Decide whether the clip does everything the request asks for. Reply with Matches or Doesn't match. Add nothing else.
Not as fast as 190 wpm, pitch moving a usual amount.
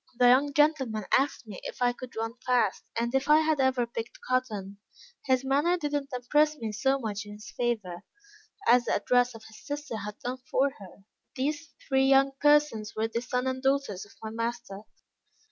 Doesn't match